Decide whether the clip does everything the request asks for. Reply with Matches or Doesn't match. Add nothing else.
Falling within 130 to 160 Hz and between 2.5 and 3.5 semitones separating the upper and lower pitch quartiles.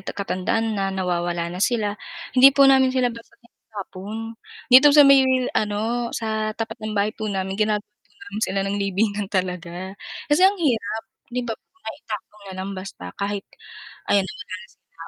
Doesn't match